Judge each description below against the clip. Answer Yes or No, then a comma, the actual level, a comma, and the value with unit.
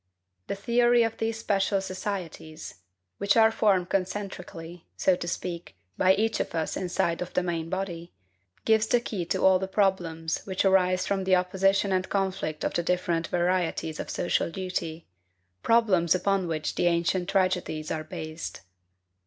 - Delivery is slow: No, average, 160 wpm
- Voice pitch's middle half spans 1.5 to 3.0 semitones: Yes, narrow, 2.5 semitones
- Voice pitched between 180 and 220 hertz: Yes, medium, 185 Hz